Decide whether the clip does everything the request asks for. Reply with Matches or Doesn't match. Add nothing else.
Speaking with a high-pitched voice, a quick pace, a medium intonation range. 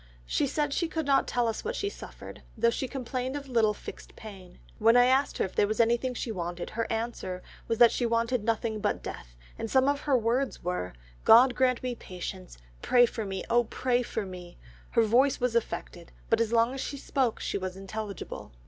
Matches